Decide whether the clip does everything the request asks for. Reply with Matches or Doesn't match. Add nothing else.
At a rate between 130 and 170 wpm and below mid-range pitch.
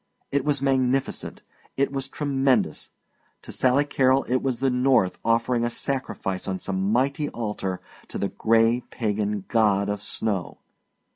Matches